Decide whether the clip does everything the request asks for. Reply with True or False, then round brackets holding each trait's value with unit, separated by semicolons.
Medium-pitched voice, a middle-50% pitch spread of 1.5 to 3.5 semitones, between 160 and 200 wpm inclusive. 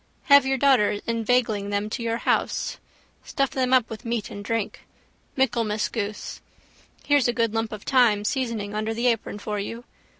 False (230 Hz; 3.0 semitones; 170 wpm)